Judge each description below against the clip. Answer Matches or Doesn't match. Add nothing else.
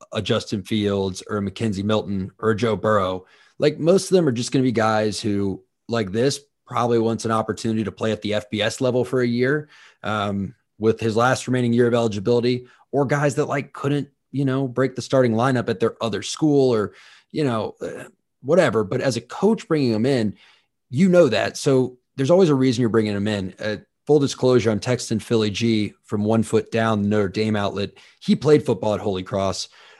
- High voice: Doesn't match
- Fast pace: Matches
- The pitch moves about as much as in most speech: Matches